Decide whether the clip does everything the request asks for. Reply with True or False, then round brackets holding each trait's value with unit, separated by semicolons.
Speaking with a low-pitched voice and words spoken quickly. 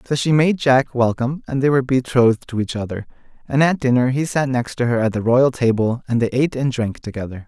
True (125 Hz; 235 wpm)